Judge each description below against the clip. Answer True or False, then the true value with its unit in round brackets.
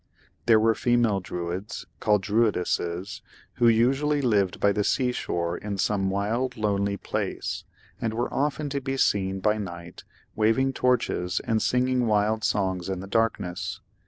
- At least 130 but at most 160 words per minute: True (150 wpm)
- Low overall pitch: True (105 Hz)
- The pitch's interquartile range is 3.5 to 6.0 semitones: True (3.9 semitones)